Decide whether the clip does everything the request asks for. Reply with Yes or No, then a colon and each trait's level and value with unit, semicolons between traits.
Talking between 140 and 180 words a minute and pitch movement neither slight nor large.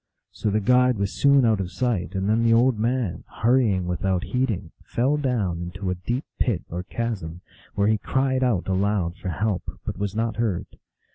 No: average, 190 wpm; average, 4.7 semitones